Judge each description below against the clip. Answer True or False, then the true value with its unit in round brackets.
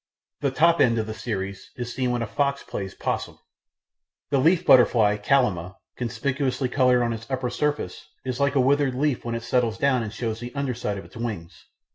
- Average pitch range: True (3.3 semitones)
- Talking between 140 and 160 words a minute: False (200 wpm)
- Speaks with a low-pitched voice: True (125 Hz)